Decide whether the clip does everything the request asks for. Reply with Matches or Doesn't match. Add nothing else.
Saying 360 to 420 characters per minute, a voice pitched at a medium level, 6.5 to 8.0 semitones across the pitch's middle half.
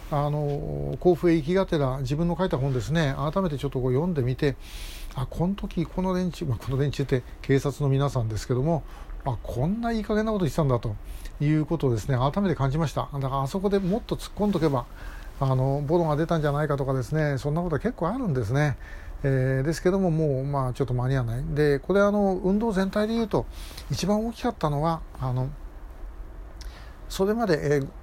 Doesn't match